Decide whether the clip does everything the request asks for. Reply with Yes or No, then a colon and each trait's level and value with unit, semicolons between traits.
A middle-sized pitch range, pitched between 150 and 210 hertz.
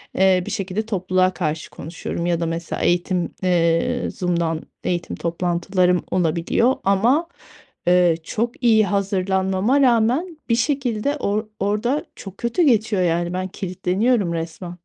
Yes: average, 4.4 semitones; high, 190 Hz